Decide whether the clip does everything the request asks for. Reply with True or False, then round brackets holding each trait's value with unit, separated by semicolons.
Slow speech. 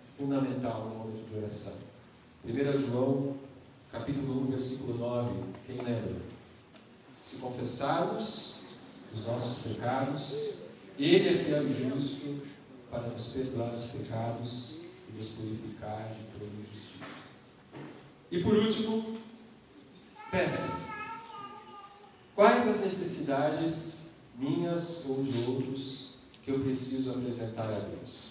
True (110 wpm)